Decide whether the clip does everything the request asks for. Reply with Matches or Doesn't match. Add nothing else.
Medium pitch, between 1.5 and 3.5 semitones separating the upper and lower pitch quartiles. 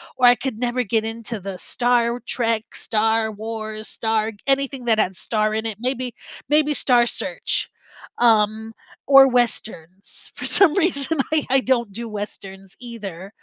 Doesn't match